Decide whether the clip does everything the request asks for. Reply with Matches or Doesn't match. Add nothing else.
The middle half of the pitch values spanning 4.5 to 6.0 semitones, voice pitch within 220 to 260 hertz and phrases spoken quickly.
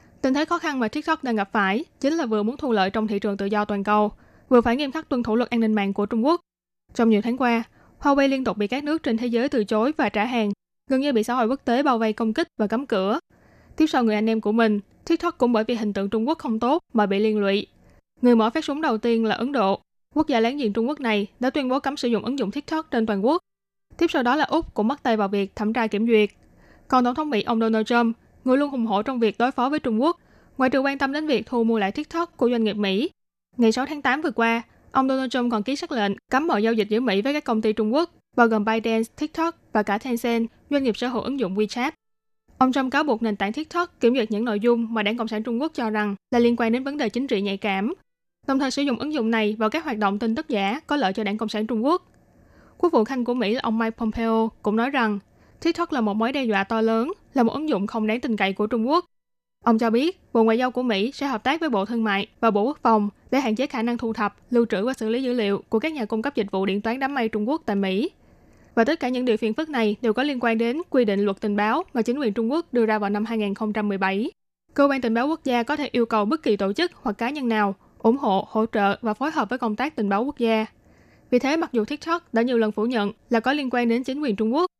Doesn't match